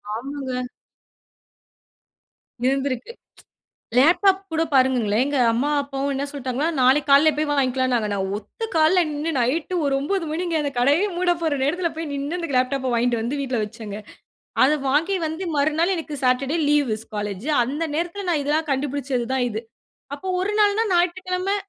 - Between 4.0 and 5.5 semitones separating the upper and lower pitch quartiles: Yes, average, 4.3 semitones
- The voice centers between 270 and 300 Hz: Yes, very high, 285 Hz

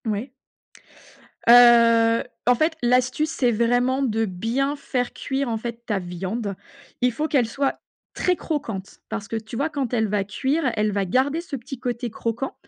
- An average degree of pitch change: Yes, average, 3.4 semitones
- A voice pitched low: No, high, 240 Hz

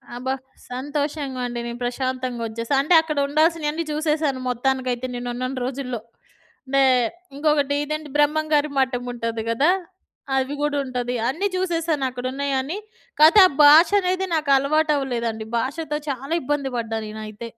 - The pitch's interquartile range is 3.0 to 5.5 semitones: Yes, average, 3.6 semitones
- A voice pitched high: Yes, very high, 275 Hz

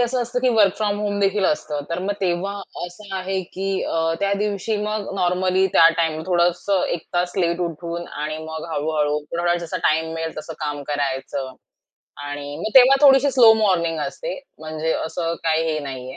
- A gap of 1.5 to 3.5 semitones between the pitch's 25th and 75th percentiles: No, average, 4.3 semitones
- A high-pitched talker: No, medium, 175 Hz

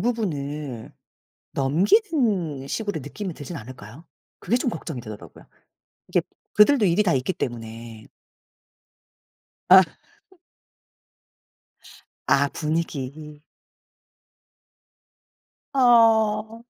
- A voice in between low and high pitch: Yes, medium, 165 Hz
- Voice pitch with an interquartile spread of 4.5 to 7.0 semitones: No, wide, 8.0 semitones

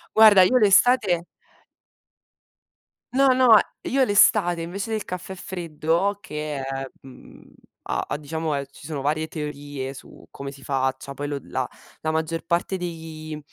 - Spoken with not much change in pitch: No, average, 5.2 semitones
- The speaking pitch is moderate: Yes, medium, 160 Hz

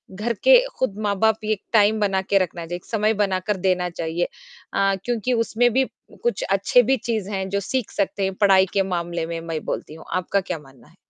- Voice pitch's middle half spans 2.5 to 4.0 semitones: Yes, average, 3.4 semitones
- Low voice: No, high, 195 Hz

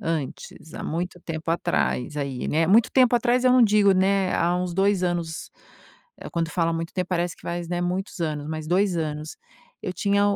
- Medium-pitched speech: Yes, medium, 175 Hz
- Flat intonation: No, average, 3.2 semitones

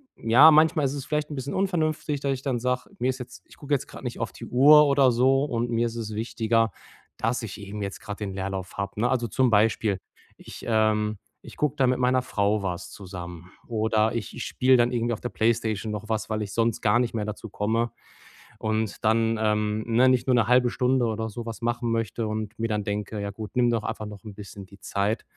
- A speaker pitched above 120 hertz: No, low, 115 Hz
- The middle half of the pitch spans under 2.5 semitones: No, average, 2.9 semitones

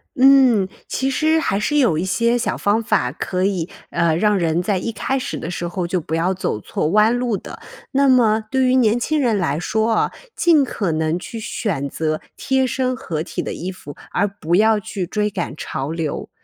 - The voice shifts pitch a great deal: Yes, wide, 6.1 semitones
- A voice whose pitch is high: Yes, high, 205 Hz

